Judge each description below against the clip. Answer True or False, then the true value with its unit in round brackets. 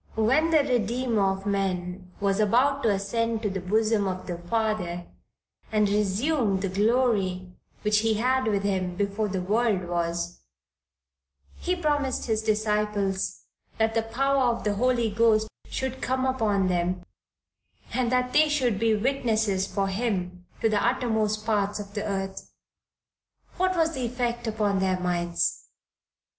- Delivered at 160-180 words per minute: False (150 wpm)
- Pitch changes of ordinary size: True (3.8 semitones)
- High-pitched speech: True (215 Hz)